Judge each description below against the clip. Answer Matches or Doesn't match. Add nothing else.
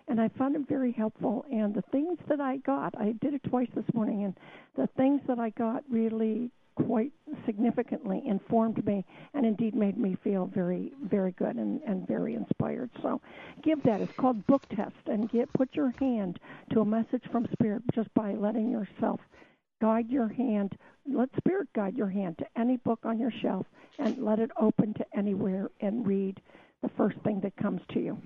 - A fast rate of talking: Doesn't match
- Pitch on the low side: Doesn't match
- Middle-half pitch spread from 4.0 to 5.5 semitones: Doesn't match